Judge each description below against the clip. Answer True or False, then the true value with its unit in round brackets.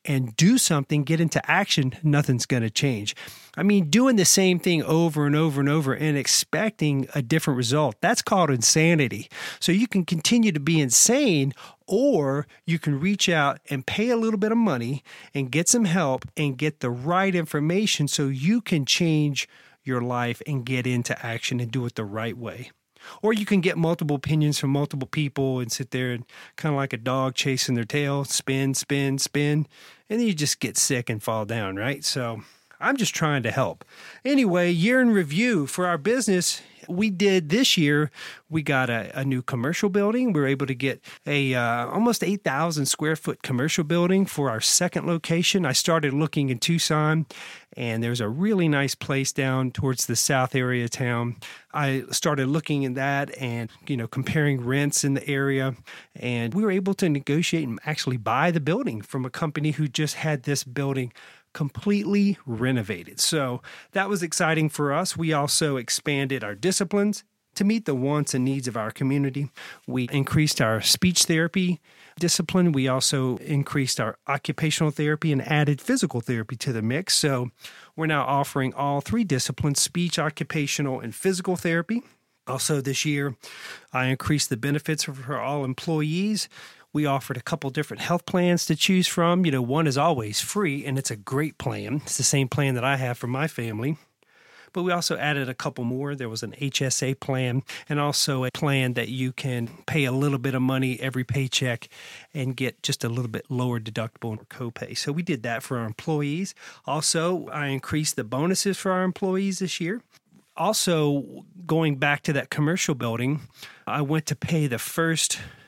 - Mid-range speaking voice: True (145 Hz)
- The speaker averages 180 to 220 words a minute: True (185 wpm)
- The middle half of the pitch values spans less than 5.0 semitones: True (4.3 semitones)